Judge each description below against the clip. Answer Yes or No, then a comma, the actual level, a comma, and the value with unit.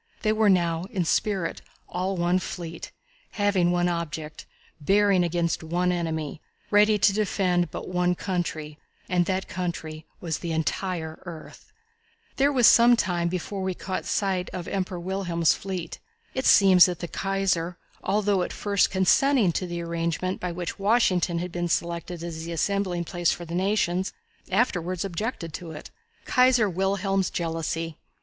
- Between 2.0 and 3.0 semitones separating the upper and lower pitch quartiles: Yes, narrow, 2.4 semitones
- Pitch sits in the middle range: Yes, medium, 180 Hz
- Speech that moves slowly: No, average, 155 wpm